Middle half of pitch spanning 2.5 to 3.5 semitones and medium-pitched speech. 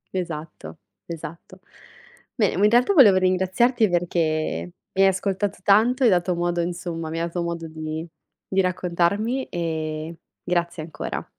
Yes: average, 2.8 semitones; medium, 175 Hz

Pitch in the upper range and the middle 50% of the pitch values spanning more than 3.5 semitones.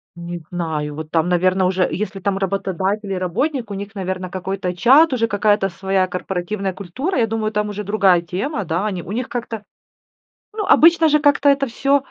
Yes: high, 195 Hz; average, 3.9 semitones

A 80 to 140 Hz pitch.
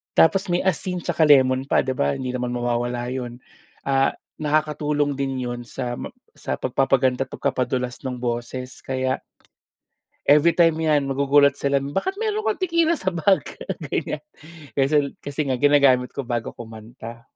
Yes: low, 135 Hz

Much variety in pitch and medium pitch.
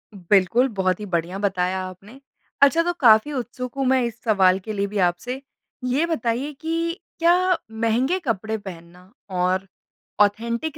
No: wide, 6.0 semitones; high, 220 Hz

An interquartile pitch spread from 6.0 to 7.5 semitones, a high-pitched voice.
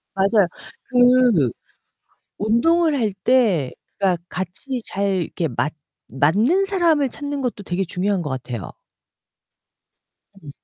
Yes: wide, 6.9 semitones; high, 205 Hz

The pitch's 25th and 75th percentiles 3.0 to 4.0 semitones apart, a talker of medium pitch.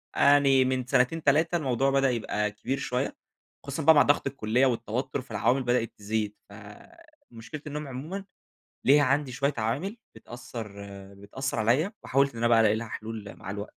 No: average, 3.7 semitones; low, 130 Hz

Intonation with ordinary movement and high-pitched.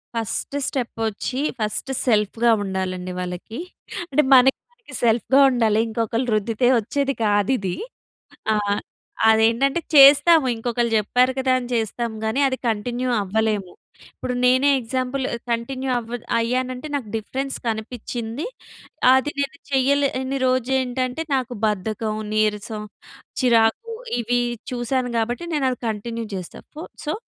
Yes: average, 3.1 semitones; high, 240 Hz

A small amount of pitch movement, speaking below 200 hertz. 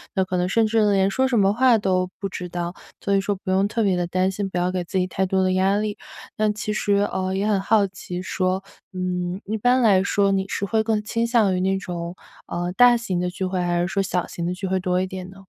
Yes: narrow, 2.1 semitones; high, 190 Hz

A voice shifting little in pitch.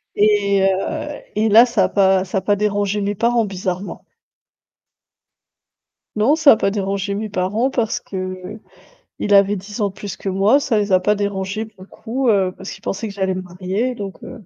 Yes: narrow, 2.1 semitones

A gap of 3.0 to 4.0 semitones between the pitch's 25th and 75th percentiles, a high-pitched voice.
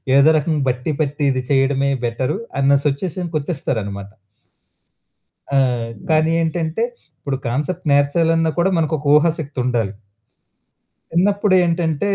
No: average, 3.3 semitones; medium, 150 Hz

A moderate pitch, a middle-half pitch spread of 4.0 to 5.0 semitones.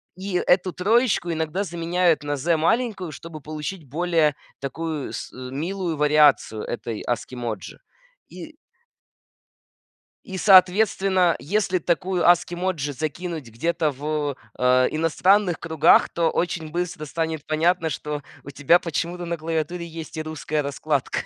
No: medium, 165 Hz; average, 3.2 semitones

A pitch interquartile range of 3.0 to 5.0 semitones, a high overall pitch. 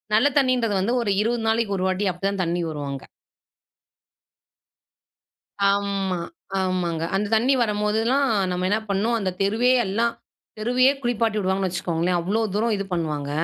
Yes: average, 3.8 semitones; high, 200 Hz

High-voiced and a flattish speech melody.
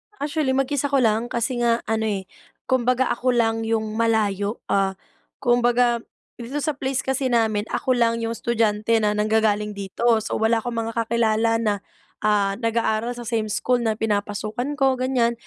Yes: high, 230 Hz; narrow, 2.1 semitones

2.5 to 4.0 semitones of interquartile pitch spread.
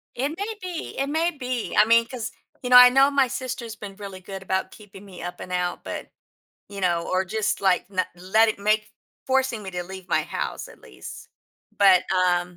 No: average, 5.0 semitones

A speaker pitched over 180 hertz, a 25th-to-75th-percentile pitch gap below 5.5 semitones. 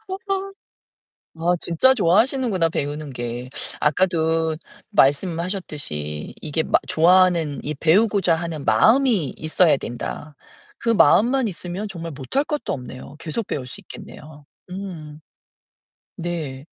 No: medium, 165 Hz; average, 5.1 semitones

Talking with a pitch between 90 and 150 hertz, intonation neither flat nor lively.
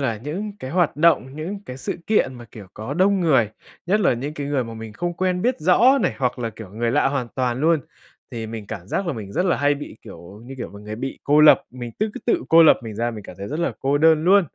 No: low, 135 Hz; wide, 6.6 semitones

